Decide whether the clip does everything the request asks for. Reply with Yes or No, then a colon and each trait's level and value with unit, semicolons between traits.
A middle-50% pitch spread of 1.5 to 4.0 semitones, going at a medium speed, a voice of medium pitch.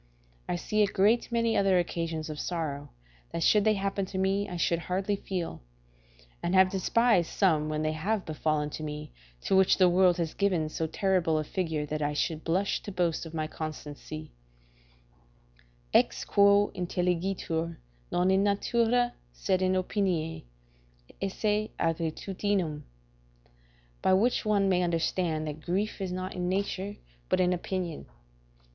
Yes: average, 3.5 semitones; average, 150 wpm; medium, 180 Hz